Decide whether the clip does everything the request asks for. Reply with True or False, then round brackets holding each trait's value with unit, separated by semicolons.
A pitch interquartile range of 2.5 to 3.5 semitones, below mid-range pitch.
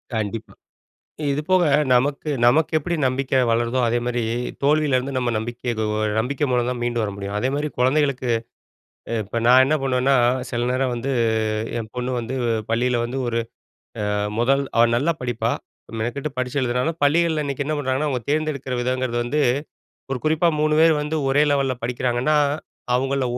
True (3.1 semitones; 130 Hz)